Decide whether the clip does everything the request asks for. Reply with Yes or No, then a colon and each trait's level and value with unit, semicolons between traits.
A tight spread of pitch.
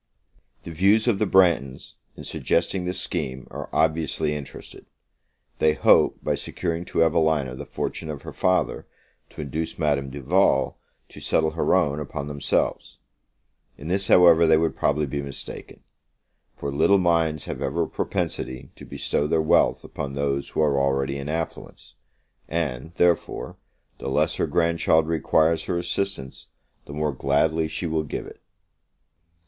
No: average, 3.0 semitones